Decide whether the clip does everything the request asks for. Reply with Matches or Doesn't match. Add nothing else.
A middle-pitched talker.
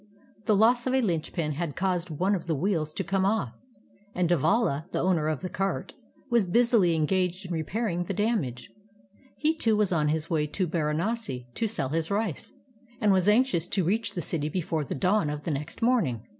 Matches